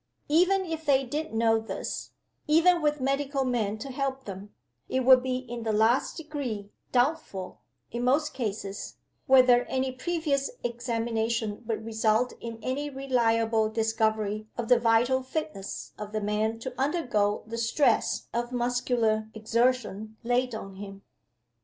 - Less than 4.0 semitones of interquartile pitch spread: Yes, average, 3.4 semitones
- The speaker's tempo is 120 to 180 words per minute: Yes, average, 140 wpm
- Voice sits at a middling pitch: No, high, 240 Hz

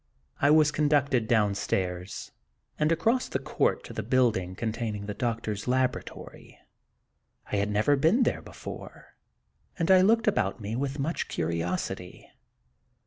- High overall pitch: No, low, 120 Hz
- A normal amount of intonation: No, wide, 6.8 semitones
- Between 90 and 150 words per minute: Yes, average, 140 wpm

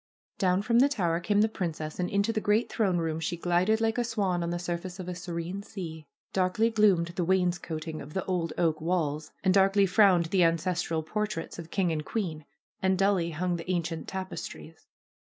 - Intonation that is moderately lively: Yes, average, 3.0 semitones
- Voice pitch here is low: No, medium, 180 Hz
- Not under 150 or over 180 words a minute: No, average, 195 wpm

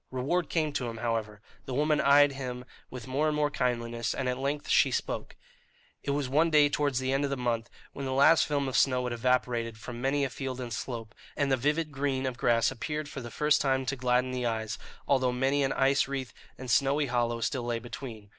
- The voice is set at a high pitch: No, low, 130 Hz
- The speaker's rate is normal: No, fast, 225 wpm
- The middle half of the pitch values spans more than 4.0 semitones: No, average, 2.7 semitones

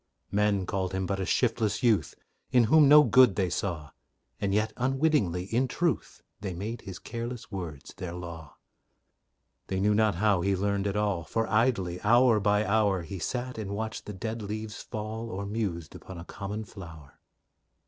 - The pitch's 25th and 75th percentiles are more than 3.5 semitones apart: No, average, 3.2 semitones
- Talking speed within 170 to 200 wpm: Yes, average, 175 wpm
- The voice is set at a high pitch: No, low, 105 Hz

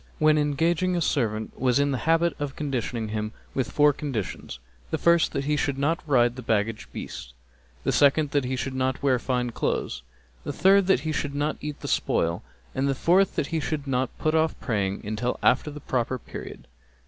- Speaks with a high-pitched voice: No, medium, 140 Hz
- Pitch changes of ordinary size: Yes, average, 3.8 semitones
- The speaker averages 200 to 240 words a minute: Yes, fast, 205 wpm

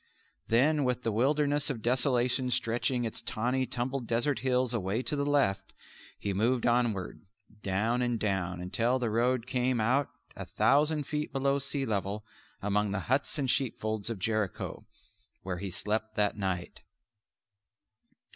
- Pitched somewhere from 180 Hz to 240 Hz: No, low, 120 Hz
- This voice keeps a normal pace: Yes, average, 145 wpm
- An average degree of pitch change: Yes, average, 3.8 semitones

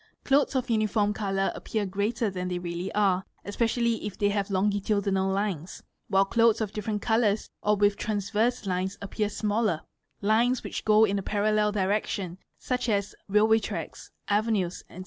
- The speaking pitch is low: No, high, 205 Hz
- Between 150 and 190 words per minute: Yes, average, 160 wpm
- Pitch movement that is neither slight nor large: No, narrow, 2.1 semitones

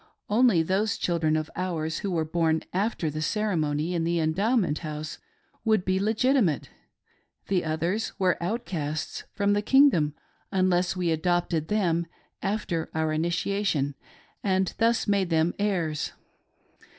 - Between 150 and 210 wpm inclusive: No, average, 140 wpm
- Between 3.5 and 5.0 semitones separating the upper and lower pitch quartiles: Yes, average, 4.1 semitones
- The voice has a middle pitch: Yes, medium, 175 Hz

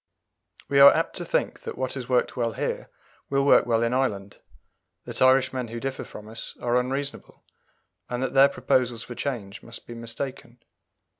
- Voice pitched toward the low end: Yes, low, 125 Hz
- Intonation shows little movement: Yes, narrow, 2.3 semitones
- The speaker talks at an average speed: Yes, average, 175 wpm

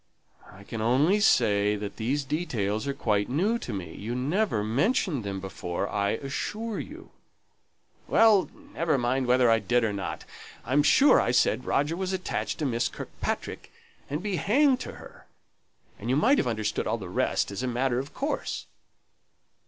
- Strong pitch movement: Yes, wide, 8.4 semitones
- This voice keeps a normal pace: Yes, average, 170 wpm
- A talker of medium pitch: No, low, 130 Hz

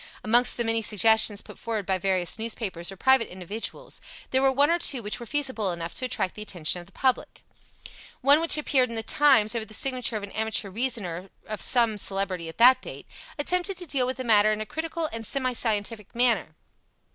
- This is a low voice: No, high, 225 Hz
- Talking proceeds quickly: Yes, fast, 210 wpm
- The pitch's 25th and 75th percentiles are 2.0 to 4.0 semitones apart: No, average, 4.5 semitones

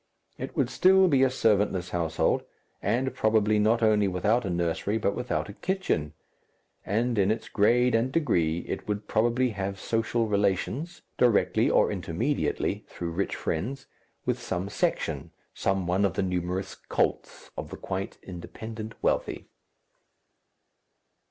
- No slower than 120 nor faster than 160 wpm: Yes, average, 140 wpm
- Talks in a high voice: No, low, 105 Hz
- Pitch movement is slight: No, average, 4.2 semitones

